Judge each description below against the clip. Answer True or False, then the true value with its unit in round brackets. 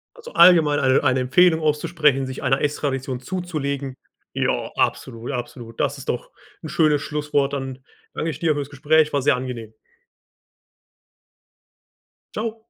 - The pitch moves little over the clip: False (3.1 semitones)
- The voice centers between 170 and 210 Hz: False (145 Hz)